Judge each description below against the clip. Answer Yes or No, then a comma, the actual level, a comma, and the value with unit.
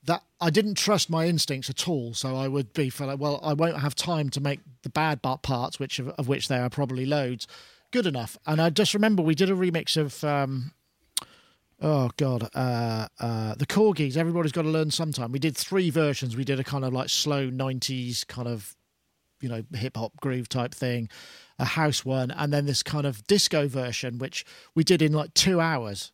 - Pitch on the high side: No, medium, 140 Hz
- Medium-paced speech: No, fast, 210 wpm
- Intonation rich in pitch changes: No, average, 3.7 semitones